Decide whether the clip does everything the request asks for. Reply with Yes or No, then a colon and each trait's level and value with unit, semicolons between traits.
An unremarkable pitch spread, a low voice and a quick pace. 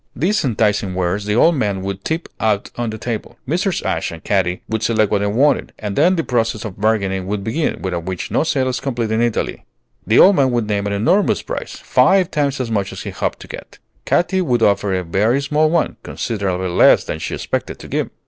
No: wide, 5.7 semitones; low, 110 Hz; fast, 225 wpm